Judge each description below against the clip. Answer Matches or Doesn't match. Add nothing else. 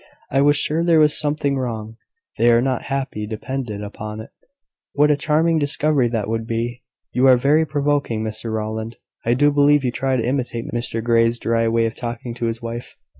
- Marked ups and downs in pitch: Doesn't match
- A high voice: Doesn't match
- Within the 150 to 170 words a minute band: Doesn't match